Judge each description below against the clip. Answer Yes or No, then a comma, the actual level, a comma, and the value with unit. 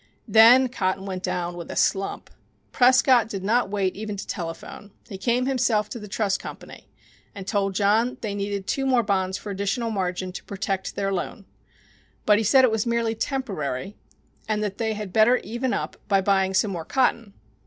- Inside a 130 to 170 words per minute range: No, average, 190 wpm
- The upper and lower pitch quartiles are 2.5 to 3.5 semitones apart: Yes, average, 3.2 semitones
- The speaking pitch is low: No, high, 205 Hz